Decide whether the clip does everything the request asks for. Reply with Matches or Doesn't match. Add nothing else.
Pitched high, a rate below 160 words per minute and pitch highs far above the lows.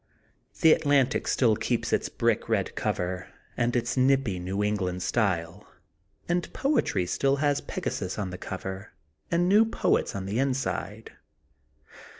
Doesn't match